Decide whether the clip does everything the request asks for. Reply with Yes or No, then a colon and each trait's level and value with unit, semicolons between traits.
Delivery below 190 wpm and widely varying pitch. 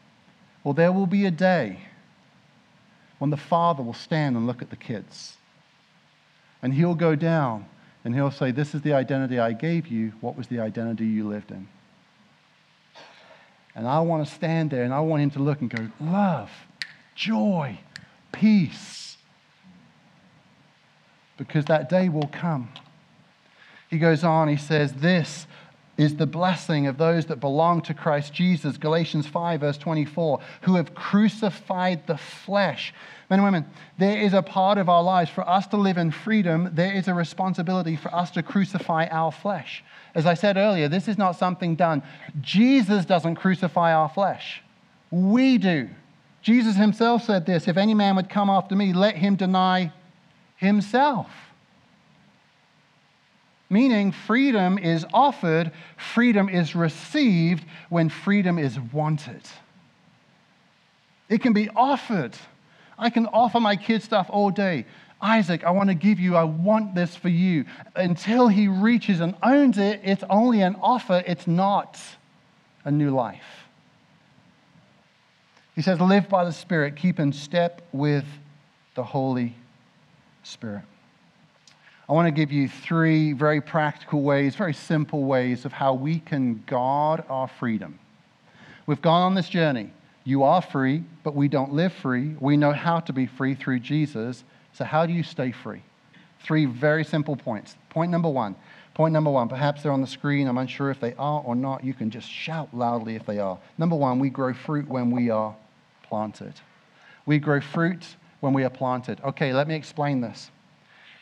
No: average, 160 wpm; average, 4.7 semitones